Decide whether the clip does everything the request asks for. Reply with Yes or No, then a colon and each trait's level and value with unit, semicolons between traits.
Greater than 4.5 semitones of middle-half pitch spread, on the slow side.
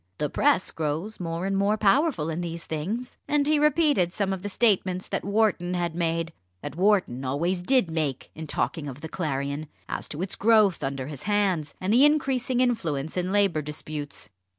No: wide, 5.5 semitones; average, 180 wpm